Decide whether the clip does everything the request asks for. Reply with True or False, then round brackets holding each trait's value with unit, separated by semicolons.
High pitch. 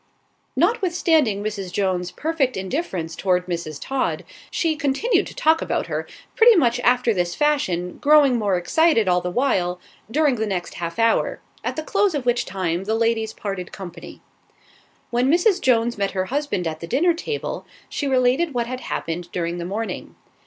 True (230 Hz)